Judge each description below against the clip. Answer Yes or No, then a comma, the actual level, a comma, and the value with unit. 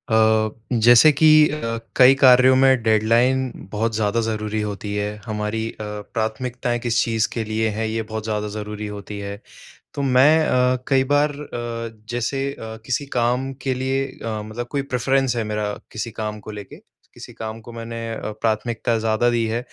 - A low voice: Yes, low, 115 Hz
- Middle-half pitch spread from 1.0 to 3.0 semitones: Yes, average, 2.7 semitones